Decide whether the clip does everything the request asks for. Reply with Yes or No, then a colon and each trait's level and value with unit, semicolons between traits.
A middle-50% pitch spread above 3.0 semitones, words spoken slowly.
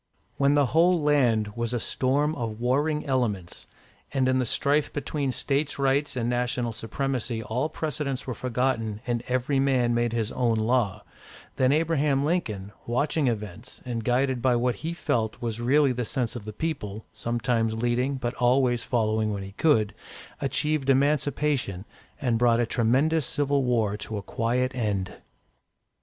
No: average, 3.4 semitones; average, 160 wpm